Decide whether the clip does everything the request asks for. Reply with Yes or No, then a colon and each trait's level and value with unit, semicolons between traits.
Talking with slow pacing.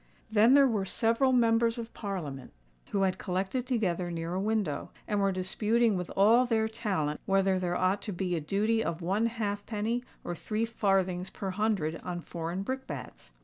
No: average, 180 wpm